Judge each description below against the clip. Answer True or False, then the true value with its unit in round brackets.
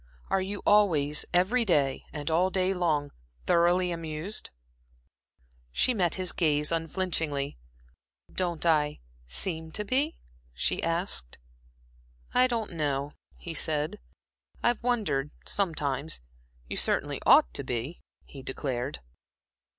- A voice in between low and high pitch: True (165 Hz)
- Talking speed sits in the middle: False (115 wpm)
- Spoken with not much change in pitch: False (4.4 semitones)